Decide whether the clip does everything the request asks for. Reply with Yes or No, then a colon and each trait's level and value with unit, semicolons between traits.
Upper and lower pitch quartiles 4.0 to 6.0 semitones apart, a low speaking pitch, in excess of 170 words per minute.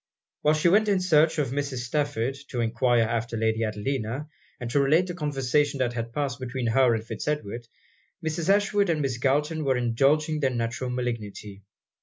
Yes: average, 4.3 semitones; low, 130 Hz; average, 180 wpm